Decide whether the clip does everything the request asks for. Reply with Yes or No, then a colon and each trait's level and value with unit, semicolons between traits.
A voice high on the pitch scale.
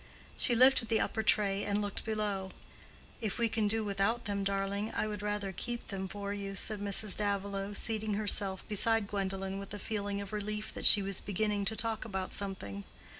Yes: high, 205 Hz